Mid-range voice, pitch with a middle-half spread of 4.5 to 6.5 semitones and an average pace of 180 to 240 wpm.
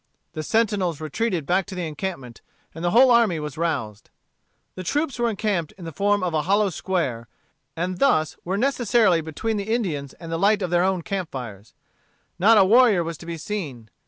Yes: medium, 180 Hz; average, 5.0 semitones; average, 195 wpm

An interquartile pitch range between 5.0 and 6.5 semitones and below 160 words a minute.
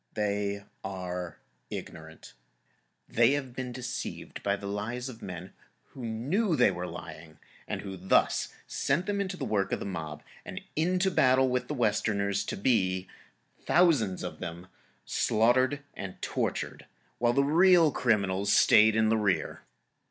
Yes: wide, 5.5 semitones; average, 145 wpm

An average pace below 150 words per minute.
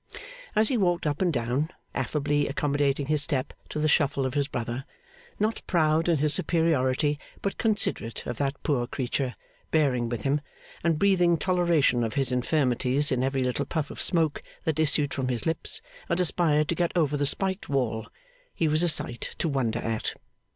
No: average, 180 wpm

